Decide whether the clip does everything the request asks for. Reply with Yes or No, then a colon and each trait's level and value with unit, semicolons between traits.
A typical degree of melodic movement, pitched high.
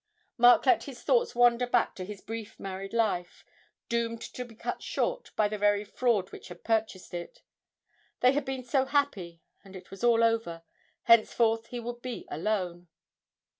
Yes: average, 3.8 semitones; high, 225 Hz